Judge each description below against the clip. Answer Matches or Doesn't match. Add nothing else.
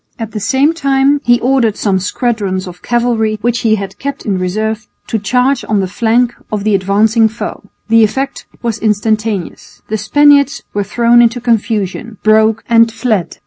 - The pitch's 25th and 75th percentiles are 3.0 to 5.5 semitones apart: Doesn't match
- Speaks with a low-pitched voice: Doesn't match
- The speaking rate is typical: Matches